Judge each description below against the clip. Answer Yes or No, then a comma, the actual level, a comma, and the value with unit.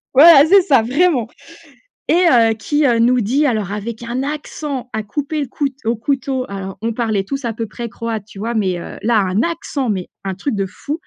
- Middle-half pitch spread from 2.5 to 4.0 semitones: No, average, 4.5 semitones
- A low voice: No, high, 235 Hz